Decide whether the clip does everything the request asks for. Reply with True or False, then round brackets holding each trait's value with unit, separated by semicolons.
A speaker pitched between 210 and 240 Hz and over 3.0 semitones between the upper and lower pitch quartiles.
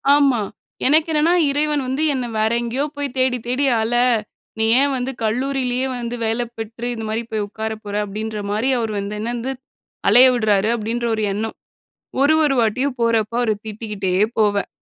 True (235 Hz; 3.4 semitones)